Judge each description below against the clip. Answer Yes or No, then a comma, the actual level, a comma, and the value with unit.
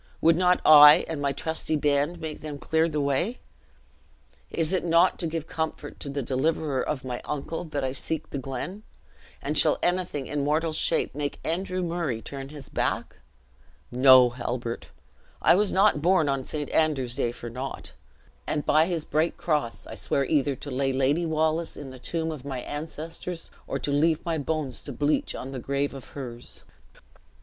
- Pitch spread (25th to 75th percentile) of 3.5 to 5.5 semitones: No, average, 3.1 semitones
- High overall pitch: No, medium, 150 Hz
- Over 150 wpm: Yes, average, 180 wpm